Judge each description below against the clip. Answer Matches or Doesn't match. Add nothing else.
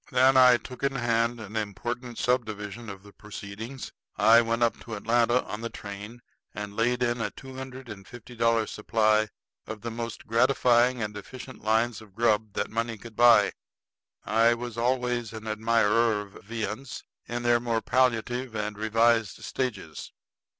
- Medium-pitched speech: Doesn't match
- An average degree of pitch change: Doesn't match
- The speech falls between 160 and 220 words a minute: Matches